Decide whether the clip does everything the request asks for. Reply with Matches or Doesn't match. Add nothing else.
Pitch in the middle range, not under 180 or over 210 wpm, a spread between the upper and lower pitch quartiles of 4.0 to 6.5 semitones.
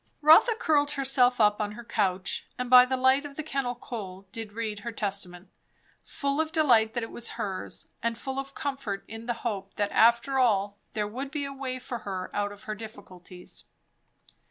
Doesn't match